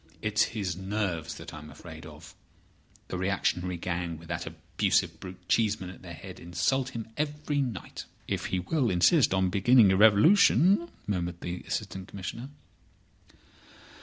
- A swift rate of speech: No, average, 150 wpm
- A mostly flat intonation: No, average, 4.8 semitones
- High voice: No, very low, 95 Hz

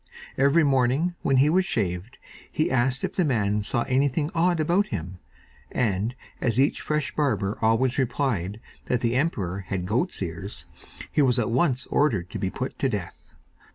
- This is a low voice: Yes, low, 125 Hz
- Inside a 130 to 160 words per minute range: No, average, 170 wpm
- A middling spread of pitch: No, wide, 5.8 semitones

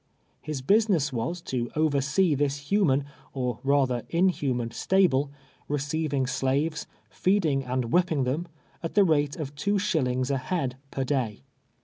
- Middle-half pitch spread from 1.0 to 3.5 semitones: No, average, 4.1 semitones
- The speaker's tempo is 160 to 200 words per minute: No, average, 140 wpm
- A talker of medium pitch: Yes, medium, 145 Hz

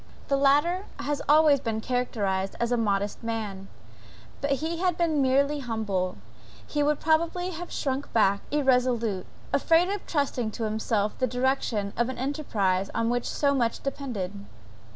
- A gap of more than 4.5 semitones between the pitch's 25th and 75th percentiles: Yes, average, 5.2 semitones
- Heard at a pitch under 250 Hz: No, very high, 255 Hz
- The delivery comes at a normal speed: Yes, average, 150 wpm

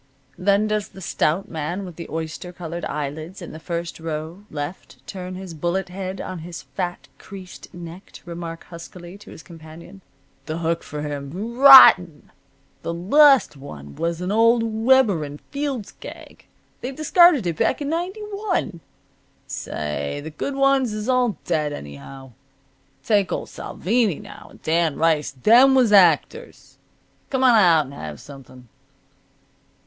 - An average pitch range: No, wide, 6.0 semitones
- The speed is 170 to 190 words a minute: No, average, 155 wpm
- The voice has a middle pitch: Yes, medium, 175 Hz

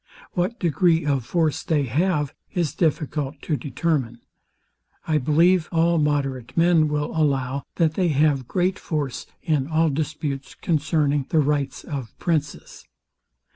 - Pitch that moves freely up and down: No, average, 2.8 semitones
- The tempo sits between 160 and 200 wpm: No, slow, 135 wpm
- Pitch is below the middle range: No, medium, 150 Hz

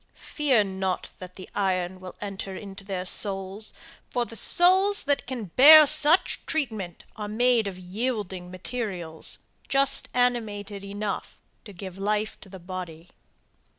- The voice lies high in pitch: Yes, high, 205 Hz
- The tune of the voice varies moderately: Yes, average, 4.7 semitones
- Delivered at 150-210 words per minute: No, average, 140 wpm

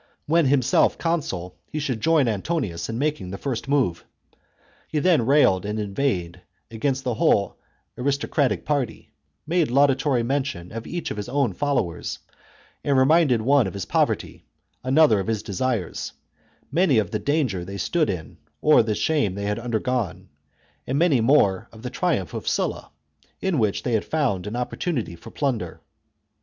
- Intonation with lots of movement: Yes, wide, 5.7 semitones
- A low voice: Yes, low, 125 Hz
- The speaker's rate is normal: Yes, average, 165 wpm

